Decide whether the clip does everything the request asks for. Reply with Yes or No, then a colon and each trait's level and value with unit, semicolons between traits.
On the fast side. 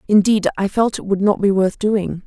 Yes: fast, 240 wpm